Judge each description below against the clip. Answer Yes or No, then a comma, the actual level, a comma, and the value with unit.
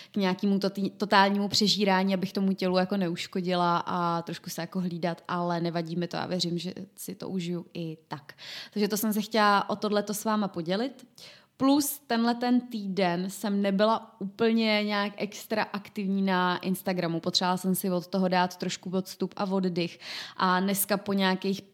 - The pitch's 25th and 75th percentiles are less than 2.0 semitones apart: No, narrow, 2.4 semitones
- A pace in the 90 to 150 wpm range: No, fast, 170 wpm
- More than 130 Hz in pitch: Yes, high, 190 Hz